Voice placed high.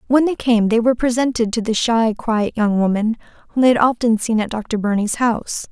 Yes: high, 230 Hz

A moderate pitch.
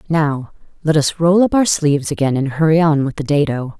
Yes: medium, 150 Hz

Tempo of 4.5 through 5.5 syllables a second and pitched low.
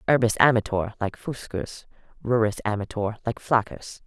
Yes: 4.9 syllables/s; low, 110 Hz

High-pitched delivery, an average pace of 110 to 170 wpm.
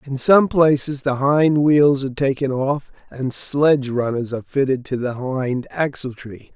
No: low, 135 Hz; average, 165 wpm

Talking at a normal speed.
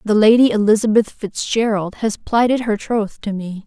Yes: average, 165 wpm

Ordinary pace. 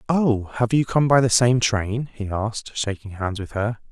No: fast, 215 wpm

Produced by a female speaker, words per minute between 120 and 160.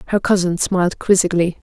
Yes: female; average, 140 wpm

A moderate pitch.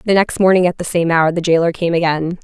Yes: medium, 170 Hz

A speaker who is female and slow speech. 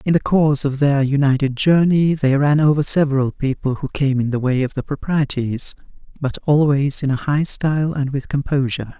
No: female; average, 195 wpm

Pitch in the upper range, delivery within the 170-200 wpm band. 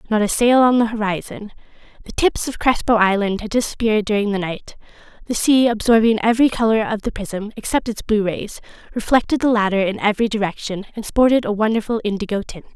Yes: high, 220 Hz; average, 190 wpm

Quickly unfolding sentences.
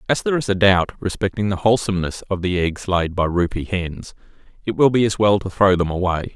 Yes: fast, 225 wpm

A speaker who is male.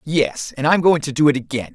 Yes: male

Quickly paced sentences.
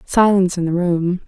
No: average, 190 wpm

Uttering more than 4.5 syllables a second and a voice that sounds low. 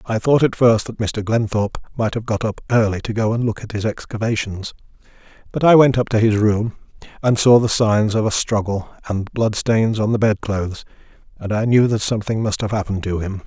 Yes: 5.5 syllables/s; low, 110 Hz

